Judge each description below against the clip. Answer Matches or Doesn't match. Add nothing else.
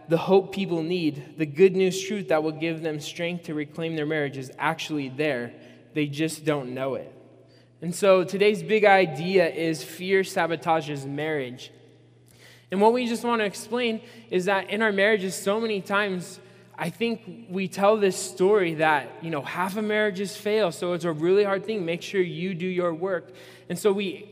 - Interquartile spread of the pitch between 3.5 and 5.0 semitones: Matches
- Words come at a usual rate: Matches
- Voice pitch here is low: Doesn't match